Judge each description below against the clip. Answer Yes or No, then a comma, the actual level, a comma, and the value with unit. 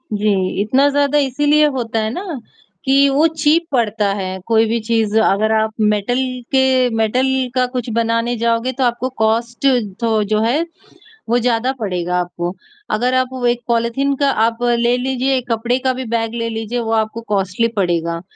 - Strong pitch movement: No, average, 2.9 semitones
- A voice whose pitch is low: No, high, 230 Hz